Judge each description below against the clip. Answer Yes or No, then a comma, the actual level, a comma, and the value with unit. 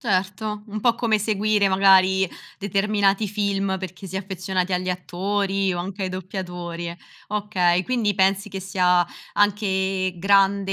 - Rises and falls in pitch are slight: Yes, narrow, 1.7 semitones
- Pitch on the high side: Yes, high, 195 Hz